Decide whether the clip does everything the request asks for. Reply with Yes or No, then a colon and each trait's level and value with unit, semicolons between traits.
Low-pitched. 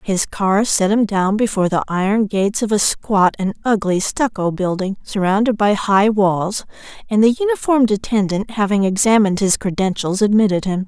No: high, 205 Hz